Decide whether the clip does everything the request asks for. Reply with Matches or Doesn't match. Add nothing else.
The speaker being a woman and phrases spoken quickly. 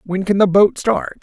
Doesn't match